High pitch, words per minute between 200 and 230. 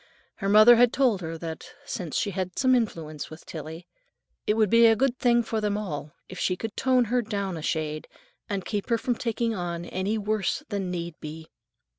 Yes: high, 200 Hz; fast, 205 wpm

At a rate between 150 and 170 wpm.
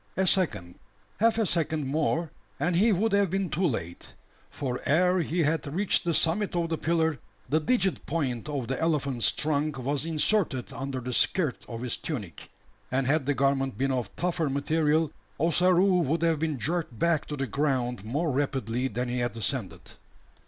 No: average, 180 wpm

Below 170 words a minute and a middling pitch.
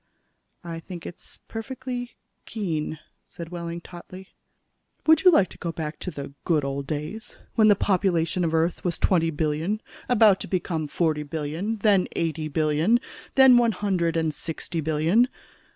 Yes: average, 160 wpm; medium, 170 Hz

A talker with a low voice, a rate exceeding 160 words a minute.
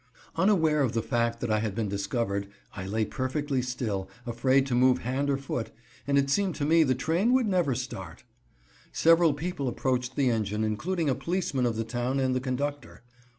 Yes: low, 130 Hz; average, 195 wpm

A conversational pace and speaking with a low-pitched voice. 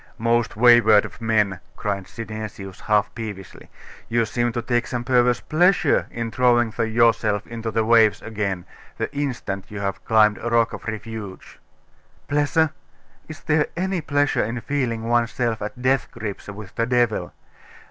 Yes: average, 150 wpm; low, 115 Hz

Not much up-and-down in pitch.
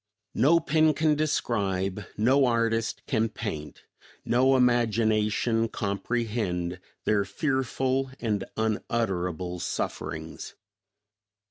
No: average, 4.5 semitones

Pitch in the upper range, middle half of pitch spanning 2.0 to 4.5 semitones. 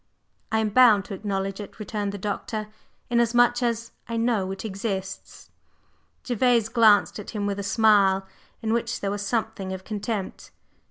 Yes: high, 210 Hz; narrow, 2.6 semitones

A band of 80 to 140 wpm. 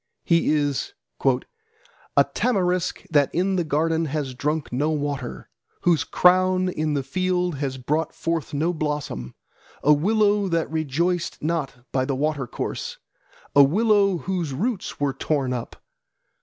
Yes: slow, 135 wpm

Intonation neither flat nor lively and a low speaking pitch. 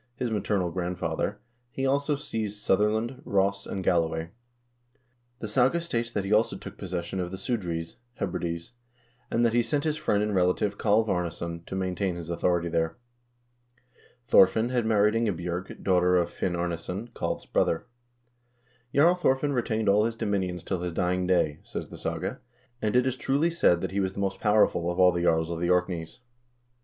Yes: average, 4.4 semitones; very low, 95 Hz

